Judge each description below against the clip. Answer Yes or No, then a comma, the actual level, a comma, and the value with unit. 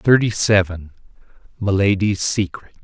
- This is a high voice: No, low, 100 Hz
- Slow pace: Yes, slow, 85 wpm